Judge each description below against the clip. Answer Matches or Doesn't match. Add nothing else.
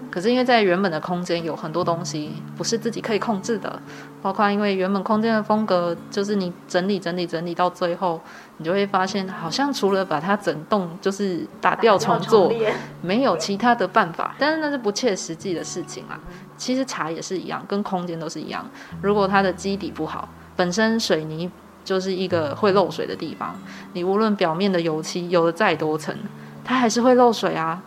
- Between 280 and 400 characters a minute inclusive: Matches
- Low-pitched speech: Doesn't match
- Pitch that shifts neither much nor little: Matches